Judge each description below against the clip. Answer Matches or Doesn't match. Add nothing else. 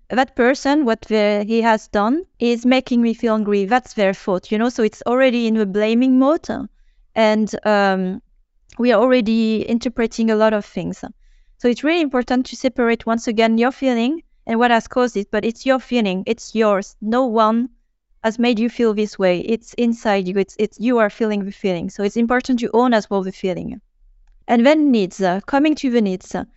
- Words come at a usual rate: Doesn't match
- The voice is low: Doesn't match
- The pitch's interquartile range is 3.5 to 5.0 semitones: Doesn't match